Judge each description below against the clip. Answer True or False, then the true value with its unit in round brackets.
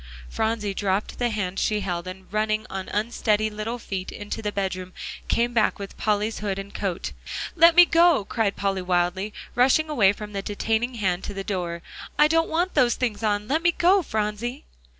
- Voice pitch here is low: False (210 Hz)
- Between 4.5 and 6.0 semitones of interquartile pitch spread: False (3.7 semitones)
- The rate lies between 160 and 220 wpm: True (190 wpm)